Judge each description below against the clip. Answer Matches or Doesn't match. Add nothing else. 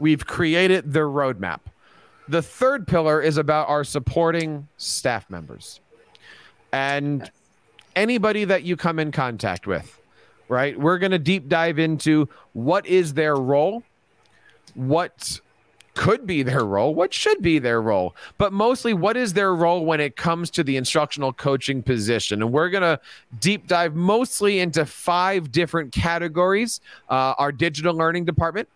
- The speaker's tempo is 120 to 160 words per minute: Matches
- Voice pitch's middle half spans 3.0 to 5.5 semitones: Matches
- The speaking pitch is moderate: Matches